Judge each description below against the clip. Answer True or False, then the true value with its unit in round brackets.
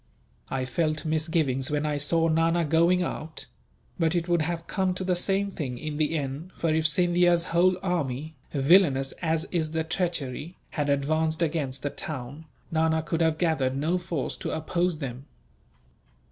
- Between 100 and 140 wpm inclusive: False (165 wpm)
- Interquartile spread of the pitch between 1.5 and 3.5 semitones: True (2.7 semitones)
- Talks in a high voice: False (160 Hz)